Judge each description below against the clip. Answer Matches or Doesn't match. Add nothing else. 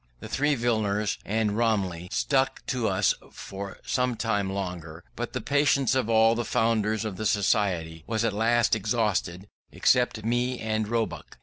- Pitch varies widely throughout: Doesn't match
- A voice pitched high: Doesn't match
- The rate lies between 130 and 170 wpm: Matches